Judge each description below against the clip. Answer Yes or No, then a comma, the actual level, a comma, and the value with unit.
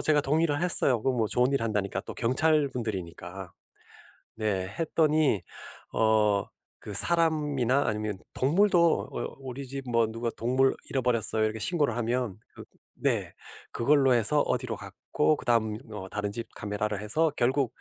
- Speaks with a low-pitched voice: Yes, low, 120 Hz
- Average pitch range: Yes, average, 5.0 semitones